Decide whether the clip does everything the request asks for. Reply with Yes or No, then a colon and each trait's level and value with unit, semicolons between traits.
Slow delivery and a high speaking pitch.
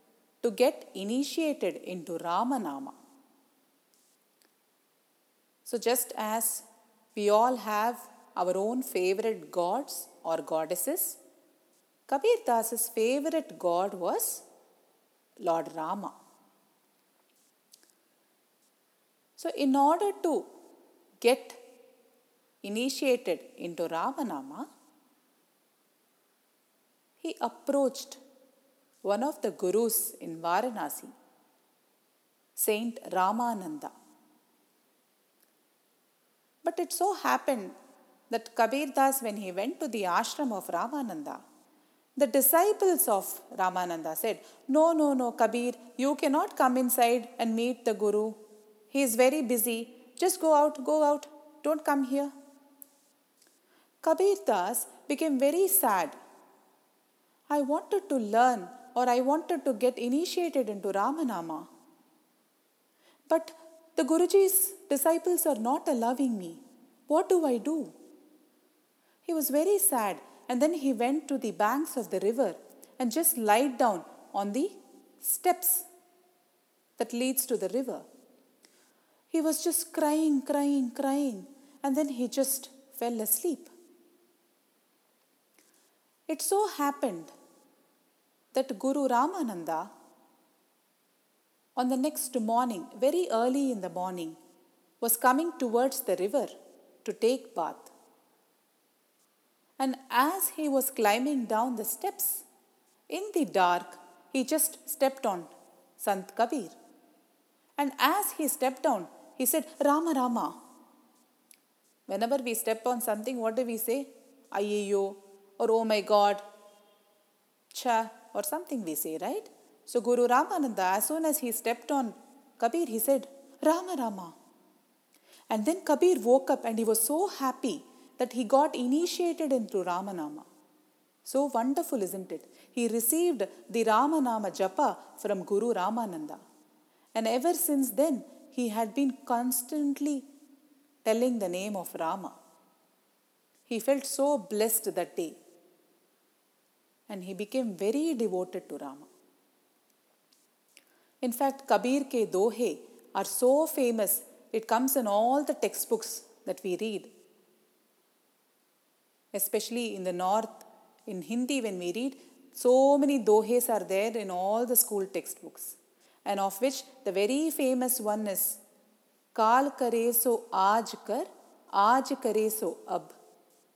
Yes: slow, 120 wpm; very high, 260 Hz